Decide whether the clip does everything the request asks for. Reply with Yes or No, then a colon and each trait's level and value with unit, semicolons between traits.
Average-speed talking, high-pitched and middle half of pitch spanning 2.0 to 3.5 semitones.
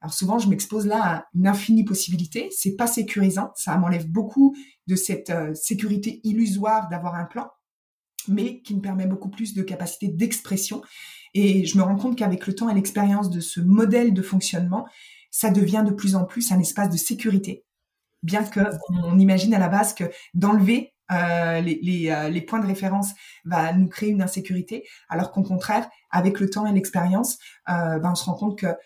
Yes: average, 195 wpm; high, 195 Hz; average, 2.9 semitones